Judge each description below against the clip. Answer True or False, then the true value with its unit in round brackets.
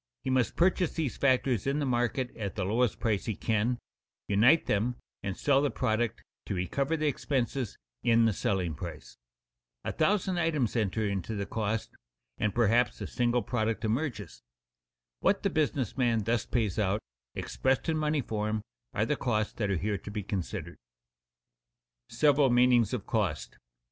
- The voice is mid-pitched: False (115 Hz)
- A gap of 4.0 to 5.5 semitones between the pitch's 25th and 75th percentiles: True (4.4 semitones)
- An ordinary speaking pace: True (170 wpm)